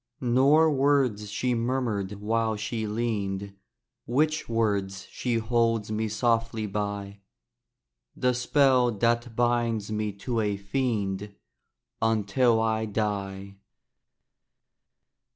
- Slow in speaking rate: Yes, slow, 100 wpm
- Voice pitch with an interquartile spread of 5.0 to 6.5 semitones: No, average, 2.8 semitones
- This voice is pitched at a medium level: No, low, 110 Hz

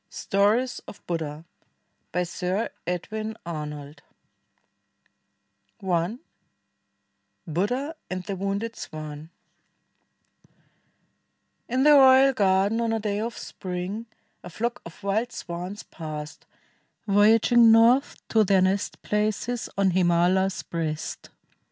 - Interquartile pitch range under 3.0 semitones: No, average, 4.5 semitones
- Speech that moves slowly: Yes, slow, 100 wpm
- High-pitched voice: Yes, high, 200 Hz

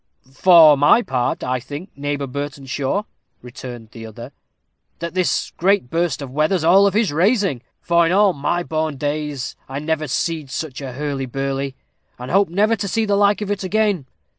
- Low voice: No, medium, 155 Hz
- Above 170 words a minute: Yes, average, 180 wpm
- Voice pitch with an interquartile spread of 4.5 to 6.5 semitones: Yes, wide, 5.6 semitones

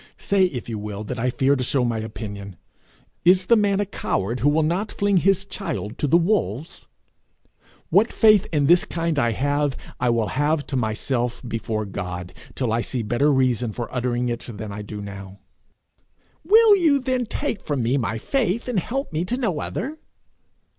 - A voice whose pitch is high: No, low, 135 Hz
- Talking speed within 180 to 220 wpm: Yes, average, 190 wpm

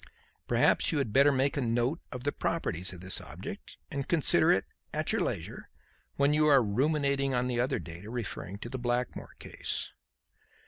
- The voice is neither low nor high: No, low, 125 Hz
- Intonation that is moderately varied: Yes, average, 3.3 semitones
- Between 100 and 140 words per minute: No, average, 180 wpm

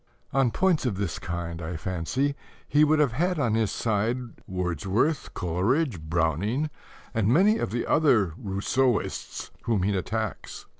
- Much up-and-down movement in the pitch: Yes, wide, 7.0 semitones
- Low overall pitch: Yes, low, 110 Hz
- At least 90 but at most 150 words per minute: Yes, average, 145 wpm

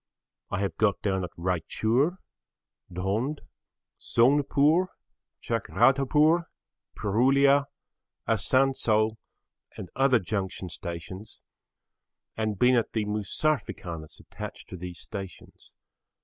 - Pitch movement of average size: No, wide, 6.2 semitones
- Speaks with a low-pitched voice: Yes, low, 110 Hz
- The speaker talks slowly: Yes, slow, 90 wpm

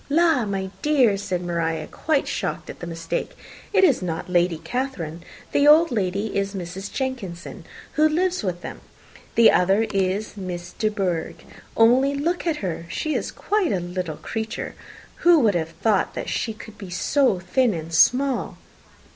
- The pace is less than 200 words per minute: Yes, average, 165 wpm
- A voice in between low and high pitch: No, high, 200 Hz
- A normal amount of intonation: No, wide, 7.2 semitones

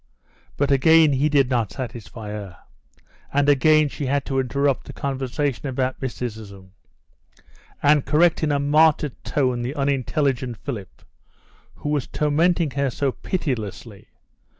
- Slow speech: Yes, slow, 130 wpm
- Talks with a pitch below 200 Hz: Yes, medium, 140 Hz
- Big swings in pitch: No, average, 3.1 semitones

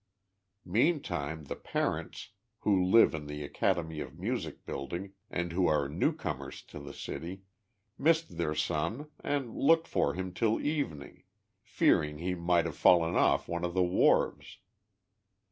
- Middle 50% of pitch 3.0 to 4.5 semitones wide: No, wide, 5.4 semitones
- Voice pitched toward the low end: Yes, very low, 85 Hz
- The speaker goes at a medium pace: Yes, average, 145 wpm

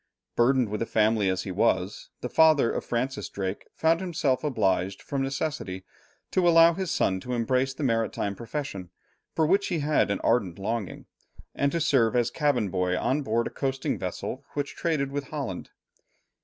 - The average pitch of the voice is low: Yes, low, 125 Hz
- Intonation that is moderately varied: No, wide, 6.3 semitones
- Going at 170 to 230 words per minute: Yes, average, 175 wpm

